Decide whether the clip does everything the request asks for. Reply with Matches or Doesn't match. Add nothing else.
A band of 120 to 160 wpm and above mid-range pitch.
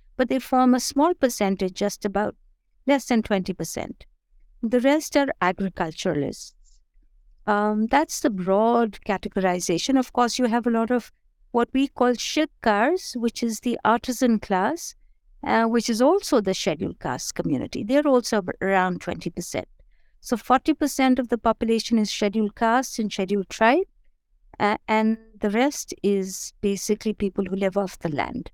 Matches